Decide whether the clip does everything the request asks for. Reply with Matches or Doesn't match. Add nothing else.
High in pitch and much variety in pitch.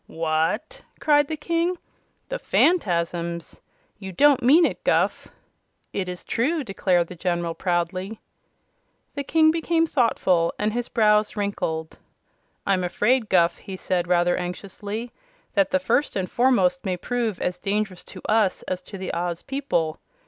Matches